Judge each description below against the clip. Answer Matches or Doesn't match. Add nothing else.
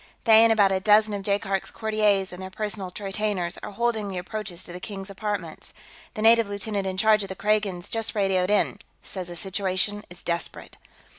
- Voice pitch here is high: Matches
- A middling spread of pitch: Doesn't match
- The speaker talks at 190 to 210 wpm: Matches